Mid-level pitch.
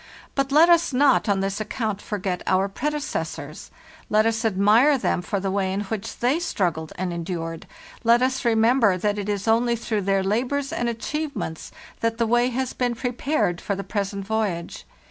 No: high, 220 Hz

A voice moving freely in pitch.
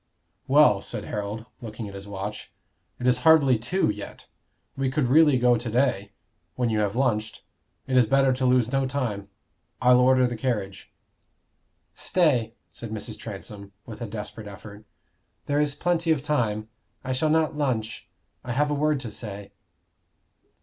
No: average, 4.2 semitones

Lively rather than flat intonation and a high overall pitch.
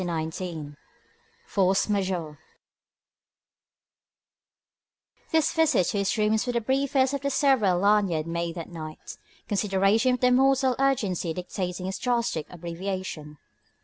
Yes: wide, 6.5 semitones; high, 195 Hz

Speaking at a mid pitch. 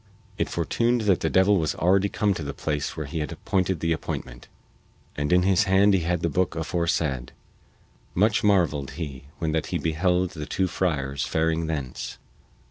No: very low, 85 Hz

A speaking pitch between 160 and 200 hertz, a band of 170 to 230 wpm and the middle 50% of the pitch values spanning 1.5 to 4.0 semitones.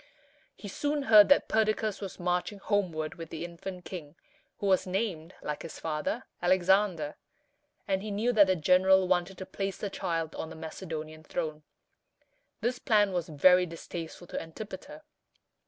No: medium, 185 Hz; average, 155 wpm; average, 3.6 semitones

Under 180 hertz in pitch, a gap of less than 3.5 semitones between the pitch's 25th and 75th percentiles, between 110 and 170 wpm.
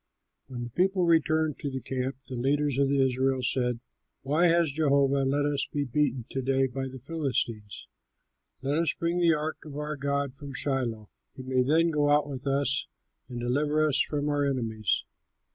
No: medium, 140 Hz; narrow, 2.4 semitones; average, 180 wpm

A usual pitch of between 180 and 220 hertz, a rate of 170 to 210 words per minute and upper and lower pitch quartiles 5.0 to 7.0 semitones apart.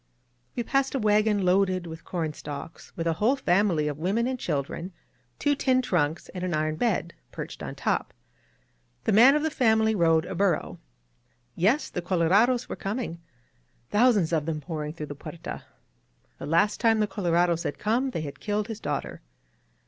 Yes: medium, 185 Hz; average, 180 wpm; average, 5.3 semitones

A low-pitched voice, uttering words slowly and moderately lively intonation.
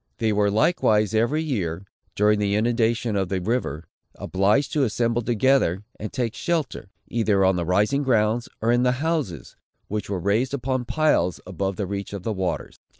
No: low, 110 Hz; average, 175 wpm; average, 4.0 semitones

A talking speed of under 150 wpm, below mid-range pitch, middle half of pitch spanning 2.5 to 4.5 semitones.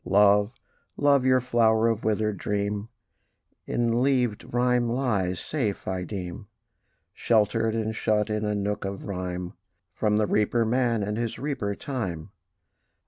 Yes: average, 140 wpm; low, 110 Hz; average, 2.9 semitones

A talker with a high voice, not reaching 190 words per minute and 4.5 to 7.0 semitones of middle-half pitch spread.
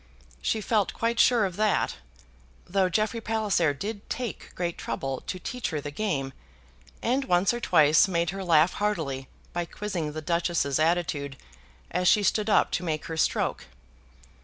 No: medium, 180 Hz; average, 160 wpm; average, 5.2 semitones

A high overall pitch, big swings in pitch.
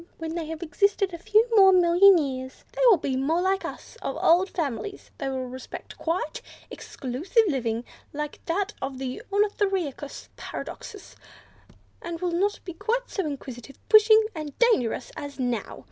Yes: very high, 330 Hz; wide, 6.4 semitones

